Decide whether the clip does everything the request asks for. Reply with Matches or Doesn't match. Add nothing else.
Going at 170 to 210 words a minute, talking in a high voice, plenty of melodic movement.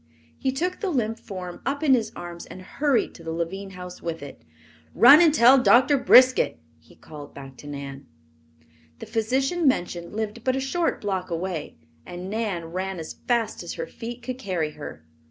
Matches